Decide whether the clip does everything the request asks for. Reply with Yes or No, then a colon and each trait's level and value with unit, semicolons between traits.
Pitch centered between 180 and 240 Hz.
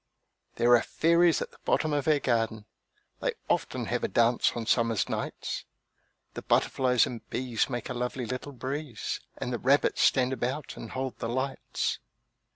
No: low, 125 Hz